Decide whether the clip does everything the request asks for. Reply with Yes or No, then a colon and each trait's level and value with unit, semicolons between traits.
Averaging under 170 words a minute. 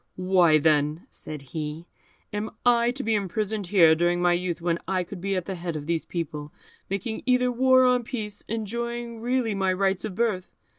No: average, 190 wpm